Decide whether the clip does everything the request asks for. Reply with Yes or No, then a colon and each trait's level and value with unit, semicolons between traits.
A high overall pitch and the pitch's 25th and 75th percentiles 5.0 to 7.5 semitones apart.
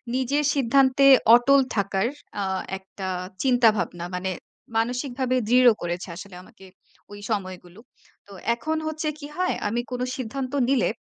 Yes: high, 240 Hz; wide, 5.5 semitones